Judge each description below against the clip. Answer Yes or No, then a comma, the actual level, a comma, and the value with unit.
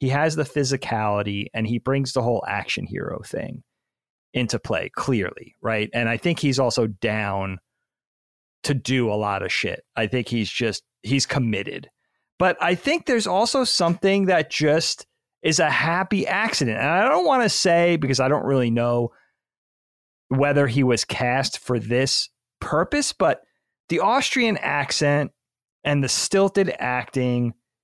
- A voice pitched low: Yes, low, 130 Hz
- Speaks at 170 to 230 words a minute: No, average, 155 wpm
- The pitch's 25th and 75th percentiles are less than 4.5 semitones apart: No, average, 4.9 semitones